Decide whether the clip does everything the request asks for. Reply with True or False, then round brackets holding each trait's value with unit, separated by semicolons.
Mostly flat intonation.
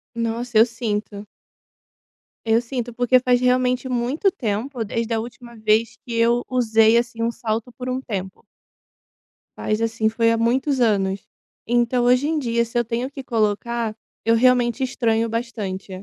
True (1.8 semitones)